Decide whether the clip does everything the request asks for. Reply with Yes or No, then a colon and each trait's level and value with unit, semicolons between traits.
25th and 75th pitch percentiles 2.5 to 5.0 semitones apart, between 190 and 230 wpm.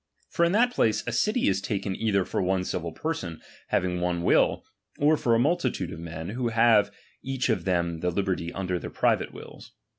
No: wide, 5.5 semitones; average, 200 wpm